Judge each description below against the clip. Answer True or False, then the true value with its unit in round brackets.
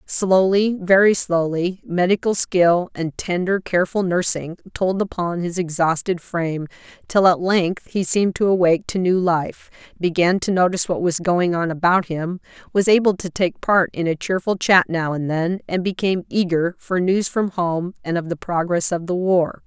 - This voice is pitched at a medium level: True (180 Hz)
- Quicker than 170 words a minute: True (180 wpm)